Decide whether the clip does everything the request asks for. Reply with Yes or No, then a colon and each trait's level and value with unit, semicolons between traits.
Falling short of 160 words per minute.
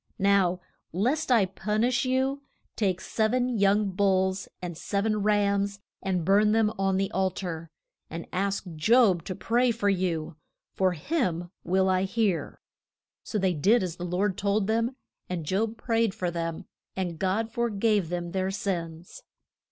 No: average, 165 wpm